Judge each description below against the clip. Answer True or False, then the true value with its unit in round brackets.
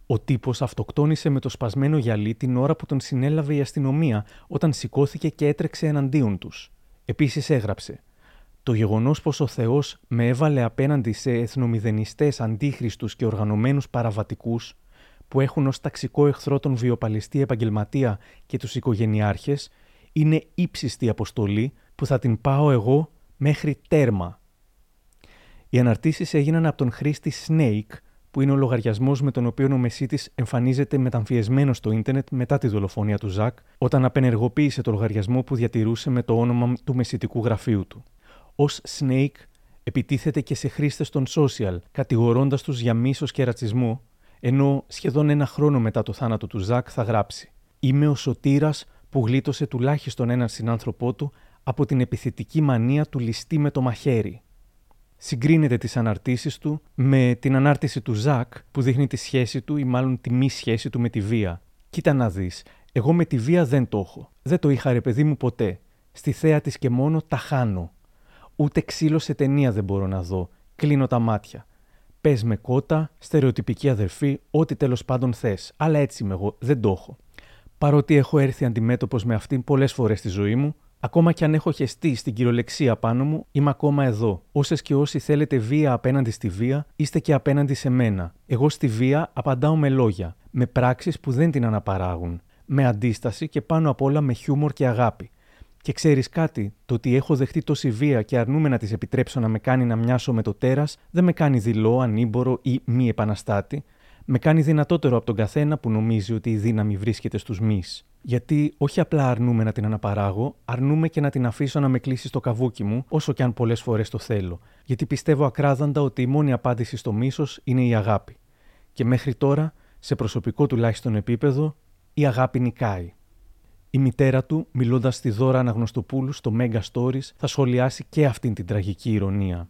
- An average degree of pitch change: True (4.0 semitones)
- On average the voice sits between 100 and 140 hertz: True (130 Hz)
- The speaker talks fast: True (175 wpm)